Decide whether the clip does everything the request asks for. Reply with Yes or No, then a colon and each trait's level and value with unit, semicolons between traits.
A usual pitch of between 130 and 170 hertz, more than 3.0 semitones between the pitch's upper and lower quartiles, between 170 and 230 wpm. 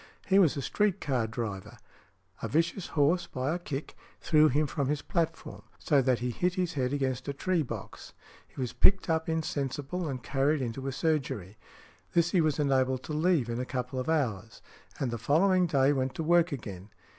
Yes: medium, 140 Hz; average, 4.2 semitones; average, 200 wpm